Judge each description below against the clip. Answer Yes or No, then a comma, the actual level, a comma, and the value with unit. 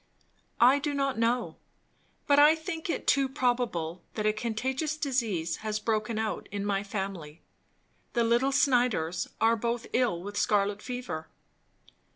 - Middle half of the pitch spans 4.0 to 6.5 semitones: Yes, average, 4.4 semitones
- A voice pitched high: Yes, high, 230 Hz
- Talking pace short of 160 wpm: Yes, average, 145 wpm